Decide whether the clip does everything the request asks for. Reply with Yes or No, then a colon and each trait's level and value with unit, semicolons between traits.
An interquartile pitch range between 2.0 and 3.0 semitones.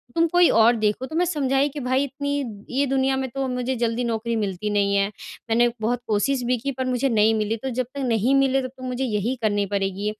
No: average, 3.6 semitones